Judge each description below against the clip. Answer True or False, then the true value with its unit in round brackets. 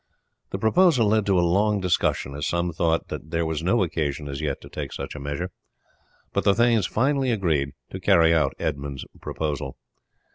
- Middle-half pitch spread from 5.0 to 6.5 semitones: True (5.6 semitones)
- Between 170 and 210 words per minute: True (185 wpm)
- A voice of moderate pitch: False (85 Hz)